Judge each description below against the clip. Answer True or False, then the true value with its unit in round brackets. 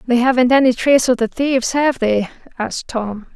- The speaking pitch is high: True (245 Hz)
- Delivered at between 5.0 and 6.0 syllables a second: True (5.6 syllables/s)